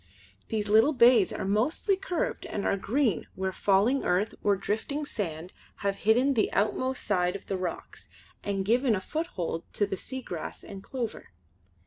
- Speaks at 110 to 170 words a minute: Yes, average, 160 wpm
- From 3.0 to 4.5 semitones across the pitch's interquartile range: No, average, 5.1 semitones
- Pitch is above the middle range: Yes, high, 210 Hz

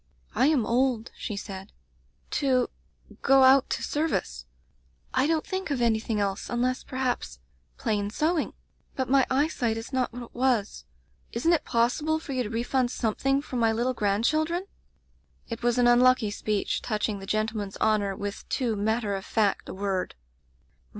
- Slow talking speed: No, average, 170 wpm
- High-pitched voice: Yes, high, 240 Hz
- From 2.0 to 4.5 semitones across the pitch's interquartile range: Yes, average, 3.9 semitones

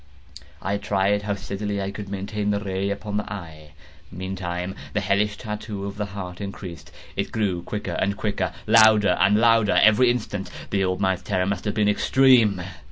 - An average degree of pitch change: No, narrow, 1.7 semitones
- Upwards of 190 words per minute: No, average, 180 wpm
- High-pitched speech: No, low, 100 Hz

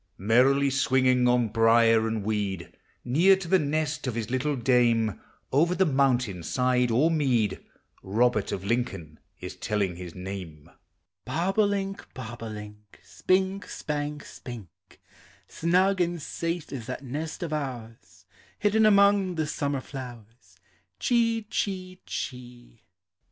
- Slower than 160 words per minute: Yes, slow, 135 wpm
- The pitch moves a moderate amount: No, wide, 6.7 semitones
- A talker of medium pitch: No, low, 130 Hz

